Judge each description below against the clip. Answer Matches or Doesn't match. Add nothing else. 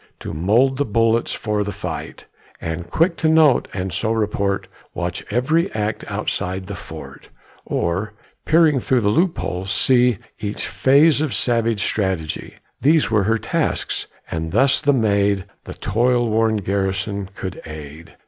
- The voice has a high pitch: Doesn't match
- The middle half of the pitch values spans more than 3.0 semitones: Matches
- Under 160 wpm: Matches